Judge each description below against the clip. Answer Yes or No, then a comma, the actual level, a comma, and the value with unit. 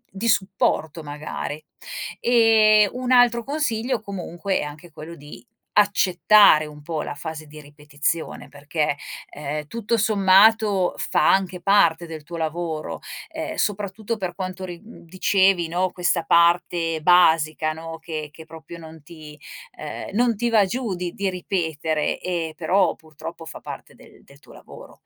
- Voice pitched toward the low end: No, medium, 175 Hz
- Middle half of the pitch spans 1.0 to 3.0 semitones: No, average, 4.2 semitones